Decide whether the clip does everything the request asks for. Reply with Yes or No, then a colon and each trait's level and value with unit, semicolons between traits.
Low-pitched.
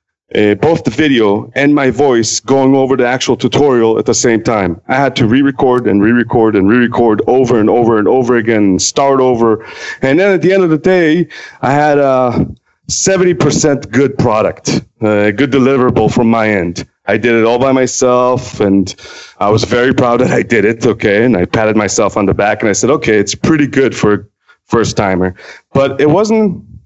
Yes: low, 125 Hz